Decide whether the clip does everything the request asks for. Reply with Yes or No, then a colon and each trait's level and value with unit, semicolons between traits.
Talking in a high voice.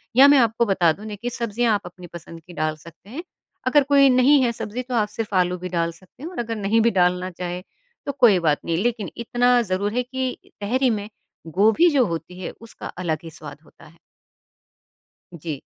Yes: high, 210 Hz